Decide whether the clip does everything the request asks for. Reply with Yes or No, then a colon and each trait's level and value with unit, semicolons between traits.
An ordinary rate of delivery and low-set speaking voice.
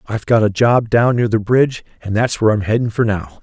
No: fast, 265 wpm; low, 110 Hz